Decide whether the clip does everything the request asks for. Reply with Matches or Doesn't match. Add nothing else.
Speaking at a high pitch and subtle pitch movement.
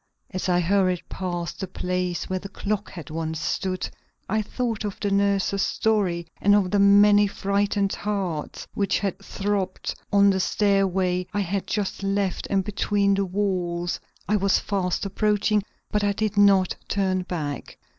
Matches